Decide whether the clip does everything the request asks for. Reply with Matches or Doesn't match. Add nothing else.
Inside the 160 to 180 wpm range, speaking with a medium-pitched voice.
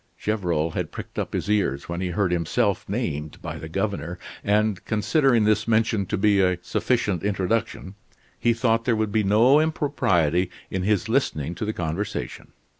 Doesn't match